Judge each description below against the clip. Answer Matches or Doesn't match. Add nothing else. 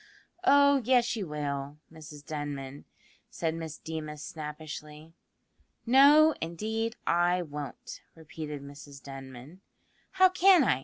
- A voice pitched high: Doesn't match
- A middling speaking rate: Doesn't match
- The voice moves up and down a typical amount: Doesn't match